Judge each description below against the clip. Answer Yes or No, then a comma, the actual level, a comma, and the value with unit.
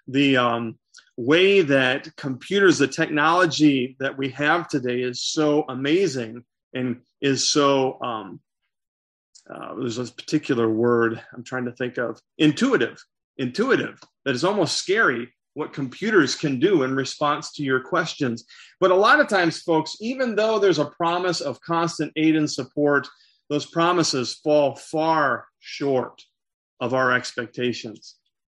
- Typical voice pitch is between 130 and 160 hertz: Yes, medium, 140 Hz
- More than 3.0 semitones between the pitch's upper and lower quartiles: Yes, average, 4.1 semitones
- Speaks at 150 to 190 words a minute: No, average, 140 wpm